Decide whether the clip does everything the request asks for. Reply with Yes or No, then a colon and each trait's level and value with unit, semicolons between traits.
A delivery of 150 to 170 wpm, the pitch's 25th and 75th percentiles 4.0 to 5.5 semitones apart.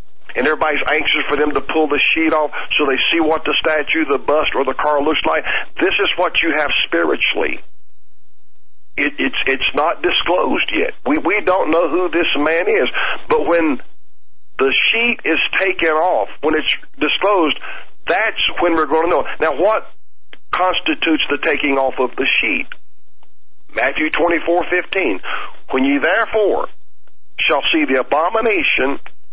No: average, 165 wpm; average, 3.4 semitones